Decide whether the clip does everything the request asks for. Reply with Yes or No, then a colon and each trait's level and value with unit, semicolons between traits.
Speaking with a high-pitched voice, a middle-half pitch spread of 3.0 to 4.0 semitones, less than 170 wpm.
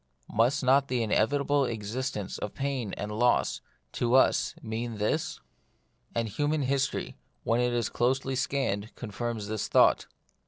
No: low, 120 Hz; average, 3.4 semitones; average, 140 wpm